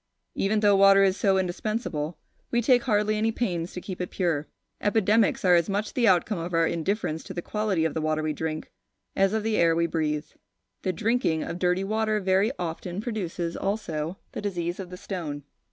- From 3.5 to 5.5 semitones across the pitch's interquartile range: Yes, average, 4.0 semitones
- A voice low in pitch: No, medium, 185 Hz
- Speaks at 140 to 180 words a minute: No, average, 200 wpm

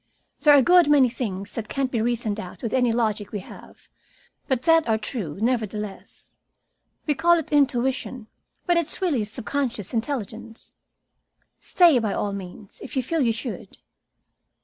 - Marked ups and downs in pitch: No, average, 4.8 semitones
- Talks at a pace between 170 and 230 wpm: No, average, 160 wpm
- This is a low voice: No, high, 240 Hz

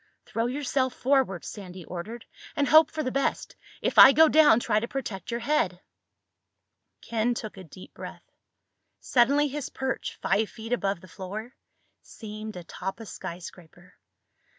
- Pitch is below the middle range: No, high, 225 Hz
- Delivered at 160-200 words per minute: No, average, 150 wpm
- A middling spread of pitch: No, wide, 5.7 semitones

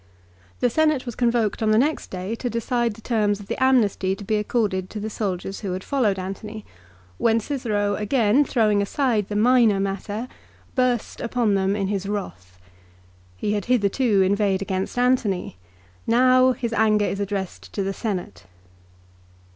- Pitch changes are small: No, average, 3.4 semitones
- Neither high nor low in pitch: No, high, 210 Hz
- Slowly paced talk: No, average, 165 wpm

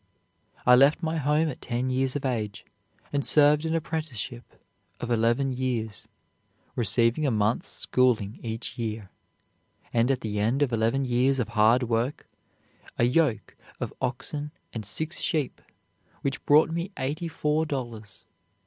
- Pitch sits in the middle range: No, low, 125 Hz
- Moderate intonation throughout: Yes, average, 4.2 semitones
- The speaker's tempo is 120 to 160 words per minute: Yes, average, 145 wpm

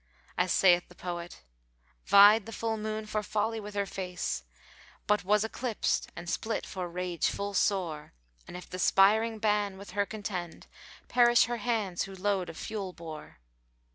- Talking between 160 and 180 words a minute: Yes, average, 170 wpm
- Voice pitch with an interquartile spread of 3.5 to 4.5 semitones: No, average, 3.1 semitones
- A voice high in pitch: Yes, high, 200 Hz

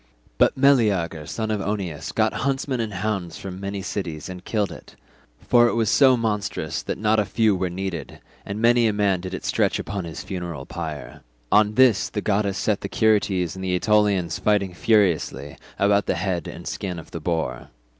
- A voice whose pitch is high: No, low, 100 Hz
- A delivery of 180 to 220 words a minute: Yes, average, 185 wpm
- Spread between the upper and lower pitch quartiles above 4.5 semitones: No, average, 3.3 semitones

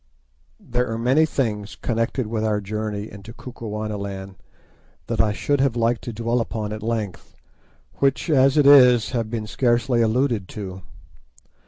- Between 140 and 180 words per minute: Yes, average, 150 wpm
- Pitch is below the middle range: Yes, low, 115 Hz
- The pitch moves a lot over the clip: No, average, 2.7 semitones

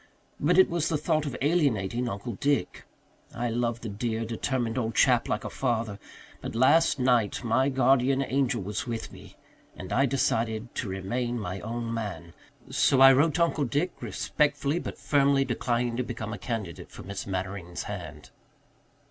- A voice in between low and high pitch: No, low, 120 Hz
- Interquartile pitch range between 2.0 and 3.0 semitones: No, average, 4.1 semitones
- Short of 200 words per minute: Yes, average, 170 wpm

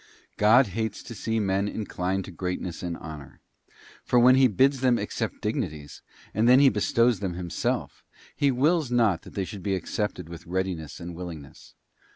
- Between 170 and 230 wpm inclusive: Yes, average, 180 wpm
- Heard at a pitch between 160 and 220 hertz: No, low, 100 Hz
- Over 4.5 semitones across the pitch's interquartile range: Yes, average, 5.3 semitones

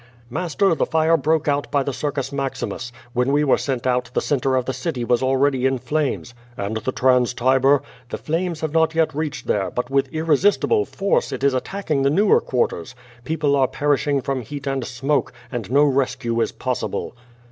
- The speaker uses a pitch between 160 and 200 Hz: No, low, 135 Hz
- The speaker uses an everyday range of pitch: Yes, average, 3.1 semitones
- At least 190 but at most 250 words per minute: Yes, average, 200 wpm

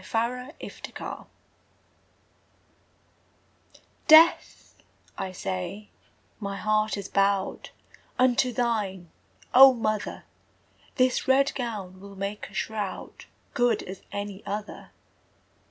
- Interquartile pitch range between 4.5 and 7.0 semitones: No, average, 3.8 semitones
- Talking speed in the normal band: No, slow, 90 wpm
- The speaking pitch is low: No, high, 210 Hz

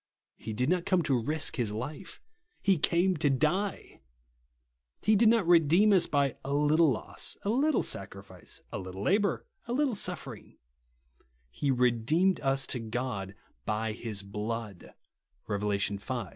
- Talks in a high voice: No, low, 135 Hz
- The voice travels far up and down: Yes, wide, 8.8 semitones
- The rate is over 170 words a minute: No, average, 150 wpm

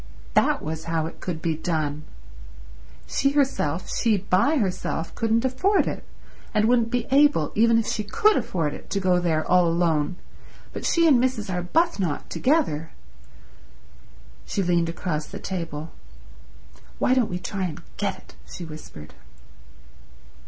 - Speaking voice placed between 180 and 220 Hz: Yes, medium, 185 Hz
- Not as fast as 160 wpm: Yes, average, 145 wpm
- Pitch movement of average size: No, wide, 6.4 semitones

